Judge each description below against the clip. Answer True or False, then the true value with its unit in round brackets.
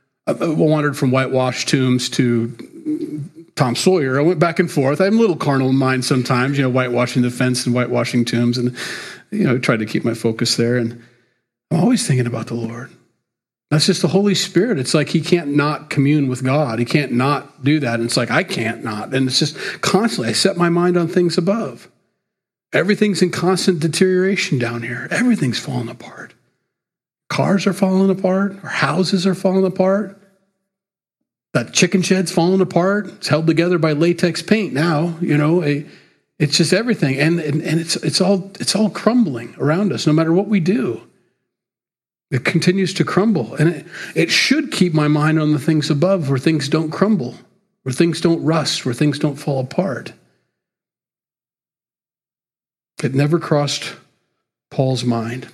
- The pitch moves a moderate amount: False (6.2 semitones)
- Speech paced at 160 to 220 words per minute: True (175 wpm)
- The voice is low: False (155 Hz)